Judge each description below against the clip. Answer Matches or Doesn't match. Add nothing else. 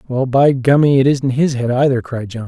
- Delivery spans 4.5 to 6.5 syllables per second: Matches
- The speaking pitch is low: Matches